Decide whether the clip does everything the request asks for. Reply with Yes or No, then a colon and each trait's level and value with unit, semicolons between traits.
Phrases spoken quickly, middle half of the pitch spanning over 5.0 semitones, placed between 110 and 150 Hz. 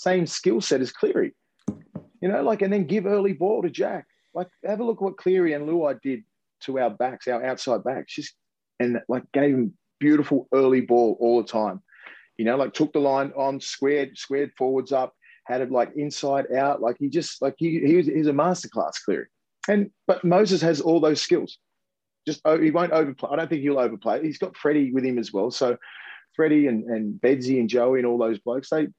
Yes: fast, 220 wpm; wide, 5.5 semitones; medium, 140 Hz